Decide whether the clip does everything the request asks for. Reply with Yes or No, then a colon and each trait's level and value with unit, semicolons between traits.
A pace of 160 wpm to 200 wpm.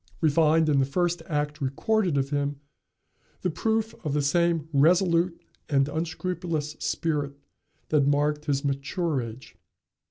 No: slow, 135 wpm